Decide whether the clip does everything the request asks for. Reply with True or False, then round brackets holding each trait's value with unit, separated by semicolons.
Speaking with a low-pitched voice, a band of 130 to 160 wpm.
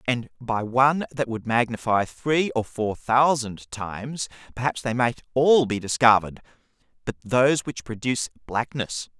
True (120 Hz; 145 wpm)